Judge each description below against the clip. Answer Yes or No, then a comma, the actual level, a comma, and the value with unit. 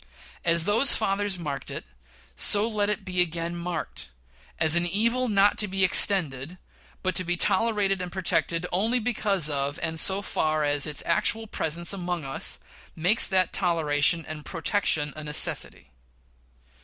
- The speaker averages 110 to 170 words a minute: Yes, average, 155 wpm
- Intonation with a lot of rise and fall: No, average, 4.3 semitones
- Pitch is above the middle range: No, medium, 180 Hz